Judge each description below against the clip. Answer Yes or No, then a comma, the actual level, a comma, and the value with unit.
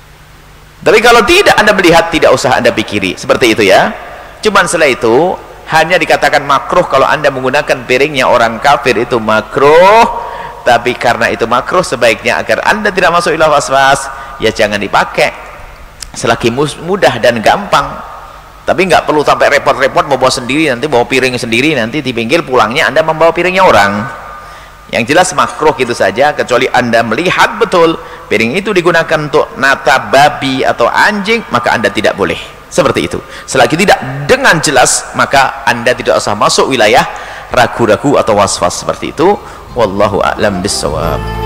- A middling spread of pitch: No, wide, 6.9 semitones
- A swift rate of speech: Yes, fast, 150 wpm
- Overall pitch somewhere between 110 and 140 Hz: Yes, low, 135 Hz